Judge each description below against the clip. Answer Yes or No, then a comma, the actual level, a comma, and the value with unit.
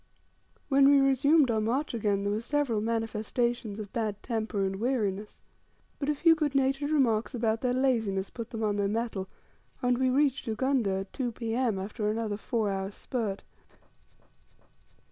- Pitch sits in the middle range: No, high, 230 Hz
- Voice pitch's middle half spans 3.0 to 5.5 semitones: Yes, average, 4.0 semitones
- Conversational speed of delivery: Yes, average, 165 wpm